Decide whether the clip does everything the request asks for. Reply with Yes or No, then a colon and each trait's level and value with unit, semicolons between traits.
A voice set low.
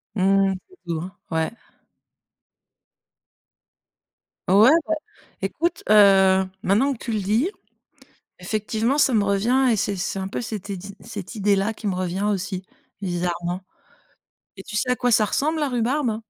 No: high, 205 Hz